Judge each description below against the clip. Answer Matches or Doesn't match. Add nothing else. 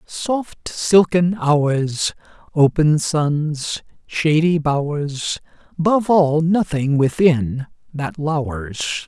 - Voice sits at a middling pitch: Matches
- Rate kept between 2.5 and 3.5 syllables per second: Matches